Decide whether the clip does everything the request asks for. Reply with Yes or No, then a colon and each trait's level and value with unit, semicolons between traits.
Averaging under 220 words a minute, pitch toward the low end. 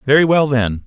Yes: fast, 205 wpm; low, 130 Hz